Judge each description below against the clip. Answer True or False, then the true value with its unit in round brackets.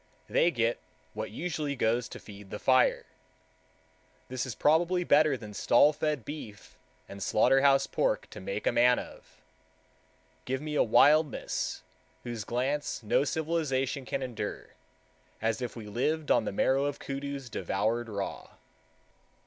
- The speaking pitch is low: True (130 Hz)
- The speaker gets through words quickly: False (140 wpm)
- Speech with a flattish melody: False (4.3 semitones)